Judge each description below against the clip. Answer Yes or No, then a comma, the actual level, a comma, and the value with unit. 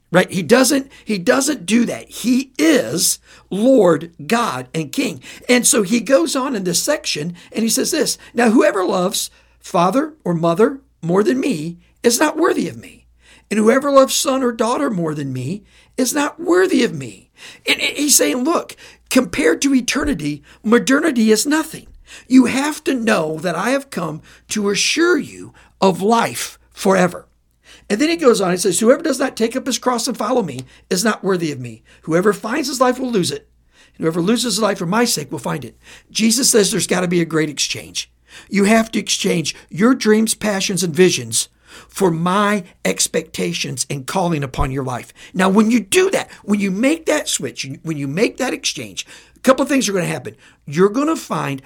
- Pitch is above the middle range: Yes, high, 215 Hz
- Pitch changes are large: Yes, wide, 7.1 semitones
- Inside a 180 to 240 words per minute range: Yes, average, 195 wpm